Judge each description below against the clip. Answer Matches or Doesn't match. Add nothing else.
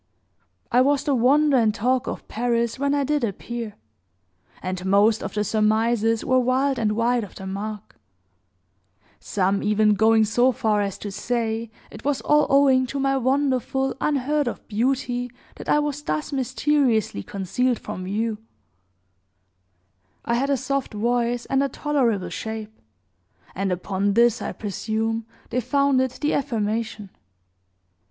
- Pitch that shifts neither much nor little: Matches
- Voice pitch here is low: Doesn't match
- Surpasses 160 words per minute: Doesn't match